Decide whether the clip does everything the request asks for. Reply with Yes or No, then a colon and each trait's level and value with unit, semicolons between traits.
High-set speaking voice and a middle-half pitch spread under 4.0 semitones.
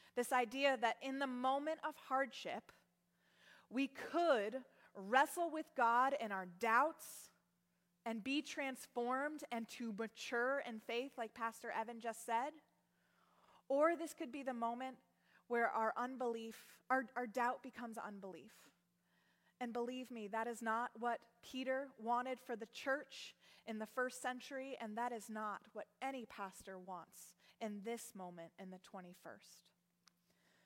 Yes: high, 240 Hz; average, 3.1 semitones